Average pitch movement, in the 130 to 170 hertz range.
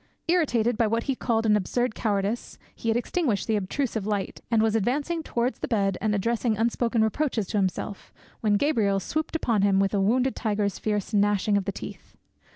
No: average, 3.0 semitones; high, 220 Hz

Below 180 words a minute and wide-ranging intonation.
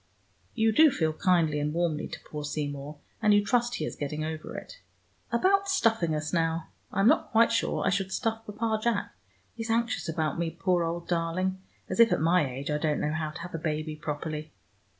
No: fast, 205 wpm; wide, 6.3 semitones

